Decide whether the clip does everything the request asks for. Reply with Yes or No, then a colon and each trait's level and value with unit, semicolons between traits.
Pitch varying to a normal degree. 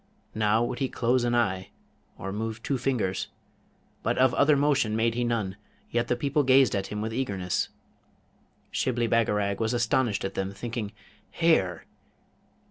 Yes: average, 3.6 semitones